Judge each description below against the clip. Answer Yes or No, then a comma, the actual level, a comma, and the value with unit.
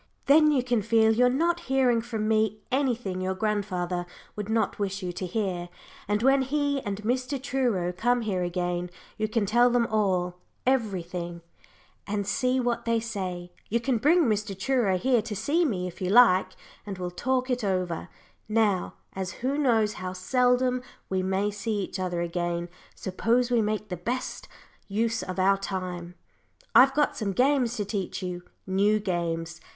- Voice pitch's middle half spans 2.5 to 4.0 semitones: No, average, 4.9 semitones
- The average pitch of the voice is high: Yes, high, 210 Hz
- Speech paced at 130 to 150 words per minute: No, average, 170 wpm